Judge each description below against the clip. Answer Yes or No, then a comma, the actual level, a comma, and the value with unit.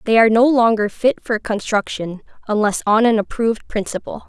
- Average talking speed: Yes, average, 170 wpm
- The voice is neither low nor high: No, high, 220 Hz